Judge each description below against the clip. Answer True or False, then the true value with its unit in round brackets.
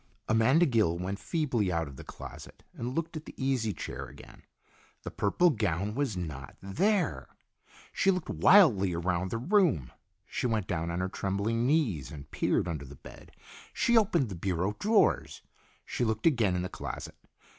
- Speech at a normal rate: True (170 wpm)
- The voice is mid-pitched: False (105 Hz)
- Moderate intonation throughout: False (8.4 semitones)